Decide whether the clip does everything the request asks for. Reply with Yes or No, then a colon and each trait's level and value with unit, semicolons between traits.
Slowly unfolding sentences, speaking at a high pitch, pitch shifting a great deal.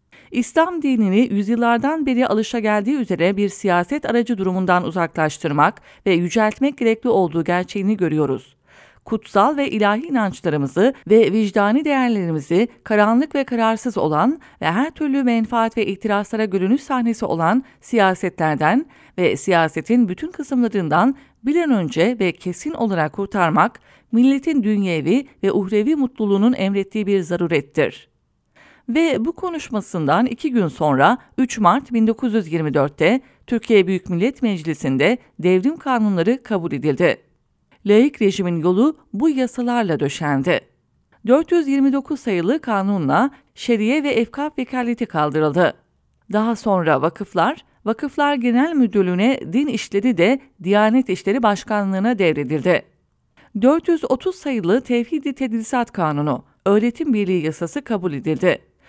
Yes: slow, 115 wpm; high, 220 Hz; wide, 5.9 semitones